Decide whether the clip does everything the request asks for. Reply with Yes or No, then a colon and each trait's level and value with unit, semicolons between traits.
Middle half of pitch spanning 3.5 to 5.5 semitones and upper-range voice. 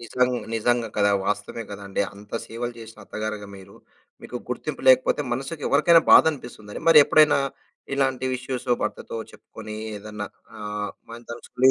No: average, 3.8 semitones; low, 115 Hz